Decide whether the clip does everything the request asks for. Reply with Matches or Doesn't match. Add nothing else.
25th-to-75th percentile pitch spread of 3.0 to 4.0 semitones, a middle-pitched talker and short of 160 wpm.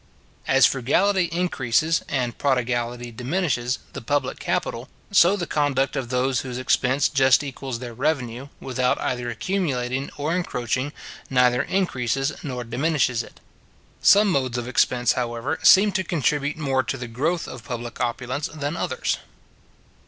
Doesn't match